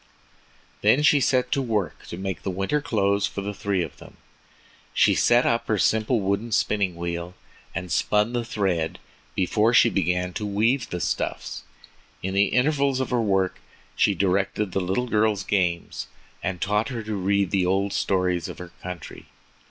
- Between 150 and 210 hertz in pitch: No, low, 100 Hz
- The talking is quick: No, average, 175 wpm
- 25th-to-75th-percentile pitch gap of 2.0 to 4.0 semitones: Yes, average, 3.6 semitones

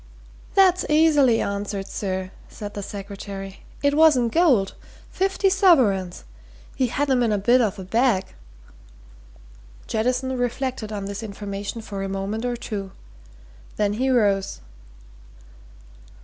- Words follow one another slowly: Yes, slow, 130 wpm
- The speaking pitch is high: Yes, high, 220 Hz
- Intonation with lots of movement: No, average, 4.7 semitones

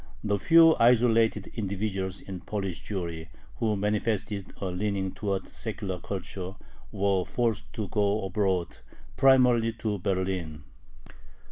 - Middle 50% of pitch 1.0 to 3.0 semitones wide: Yes, average, 2.7 semitones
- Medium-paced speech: No, slow, 115 wpm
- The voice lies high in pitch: No, low, 100 Hz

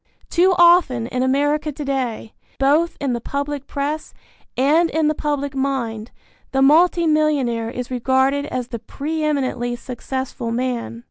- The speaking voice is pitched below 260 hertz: No, very high, 275 Hz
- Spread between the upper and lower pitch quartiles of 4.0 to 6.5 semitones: No, average, 3.4 semitones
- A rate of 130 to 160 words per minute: Yes, average, 145 wpm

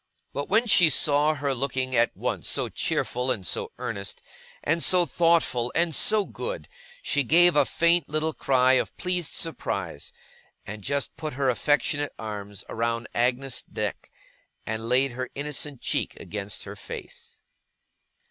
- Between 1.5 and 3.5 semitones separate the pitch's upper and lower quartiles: No, average, 5.0 semitones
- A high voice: No, low, 135 Hz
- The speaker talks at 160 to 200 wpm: No, average, 150 wpm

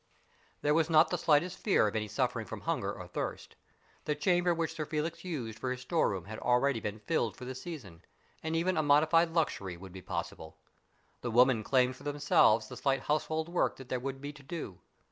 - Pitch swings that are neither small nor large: No, wide, 6.0 semitones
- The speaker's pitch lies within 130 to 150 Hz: Yes, low, 135 Hz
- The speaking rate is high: Yes, fast, 210 wpm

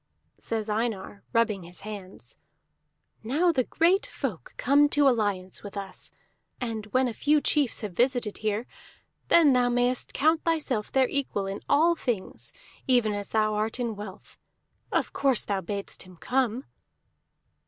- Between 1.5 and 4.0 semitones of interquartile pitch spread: No, average, 4.6 semitones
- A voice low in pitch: No, high, 230 Hz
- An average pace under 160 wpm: Yes, average, 150 wpm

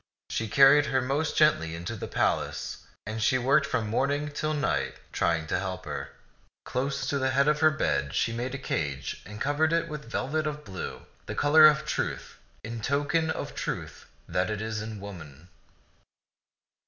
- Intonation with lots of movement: Yes, wide, 6.0 semitones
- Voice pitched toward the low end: Yes, low, 130 Hz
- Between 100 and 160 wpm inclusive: No, average, 180 wpm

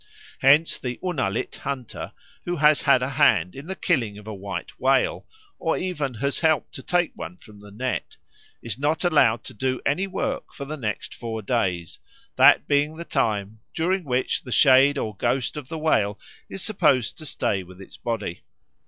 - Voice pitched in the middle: No, low, 130 Hz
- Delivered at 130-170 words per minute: No, average, 185 wpm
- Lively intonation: Yes, wide, 6.3 semitones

